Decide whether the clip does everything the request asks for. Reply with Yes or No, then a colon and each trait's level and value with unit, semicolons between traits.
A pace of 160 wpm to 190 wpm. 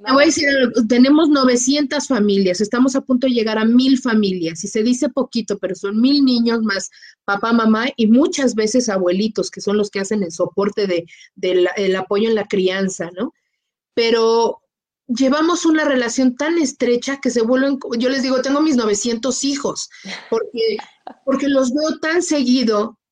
Yes: average, 170 wpm